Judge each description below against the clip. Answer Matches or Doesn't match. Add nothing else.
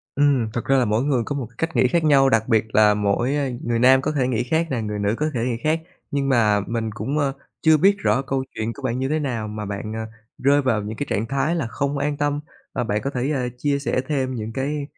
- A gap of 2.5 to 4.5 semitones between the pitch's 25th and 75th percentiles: Matches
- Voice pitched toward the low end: Matches